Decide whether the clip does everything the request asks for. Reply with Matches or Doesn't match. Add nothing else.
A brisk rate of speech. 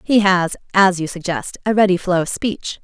Matches